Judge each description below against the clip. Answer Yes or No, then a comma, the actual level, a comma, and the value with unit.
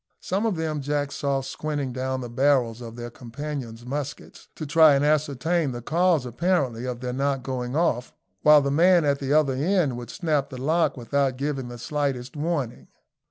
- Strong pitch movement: No, average, 3.3 semitones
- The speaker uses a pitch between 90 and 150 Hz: Yes, medium, 140 Hz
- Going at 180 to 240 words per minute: Yes, average, 185 wpm